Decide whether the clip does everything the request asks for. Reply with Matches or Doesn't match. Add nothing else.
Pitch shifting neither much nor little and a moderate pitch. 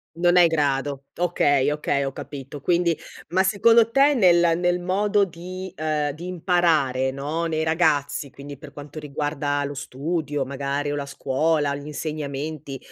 Matches